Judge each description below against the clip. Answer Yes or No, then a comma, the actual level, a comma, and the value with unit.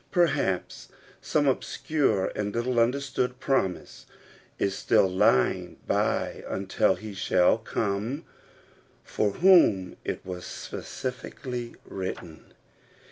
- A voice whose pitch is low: Yes, low, 110 Hz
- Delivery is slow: Yes, slow, 95 wpm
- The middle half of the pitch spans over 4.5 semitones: Yes, wide, 5.6 semitones